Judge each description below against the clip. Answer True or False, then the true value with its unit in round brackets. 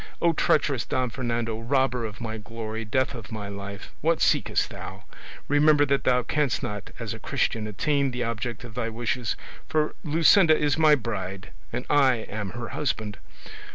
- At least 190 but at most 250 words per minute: False (170 wpm)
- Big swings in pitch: False (4.6 semitones)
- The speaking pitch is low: True (120 Hz)